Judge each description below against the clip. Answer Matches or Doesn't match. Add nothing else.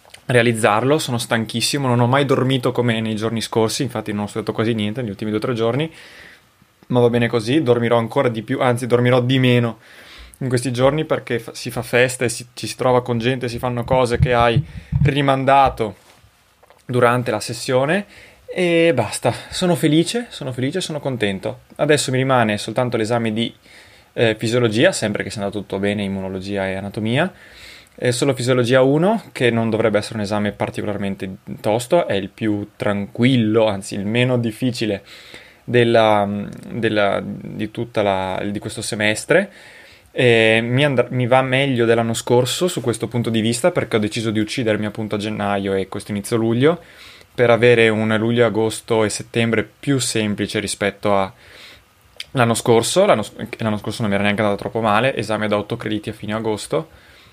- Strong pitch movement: Doesn't match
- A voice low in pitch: Matches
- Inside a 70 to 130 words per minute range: Doesn't match